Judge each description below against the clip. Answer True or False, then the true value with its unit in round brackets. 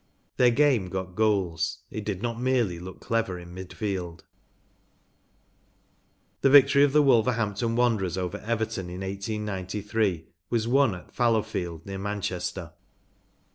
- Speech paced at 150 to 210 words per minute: False (135 wpm)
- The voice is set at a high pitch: False (105 Hz)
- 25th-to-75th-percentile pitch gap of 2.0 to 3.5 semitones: False (4.1 semitones)